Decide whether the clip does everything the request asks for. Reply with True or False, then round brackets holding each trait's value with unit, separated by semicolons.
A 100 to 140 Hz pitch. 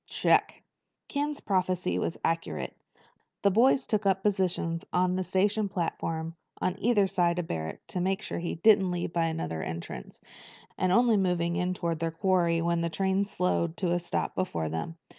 False (180 Hz)